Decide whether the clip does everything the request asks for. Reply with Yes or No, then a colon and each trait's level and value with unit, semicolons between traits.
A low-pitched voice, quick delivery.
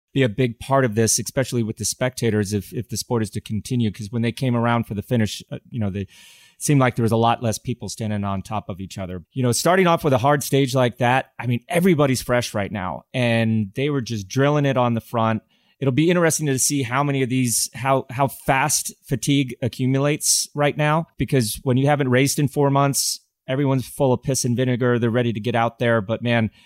Yes: low, 125 Hz; fast, 235 wpm